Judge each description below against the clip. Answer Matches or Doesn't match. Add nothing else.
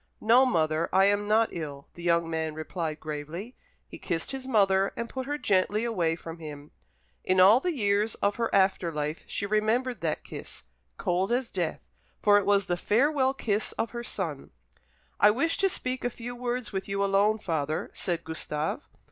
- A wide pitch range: Matches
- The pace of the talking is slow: Doesn't match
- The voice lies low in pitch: Doesn't match